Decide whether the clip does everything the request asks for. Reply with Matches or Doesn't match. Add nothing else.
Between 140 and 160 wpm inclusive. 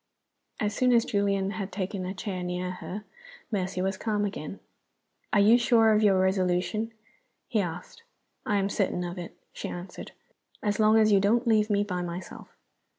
Doesn't match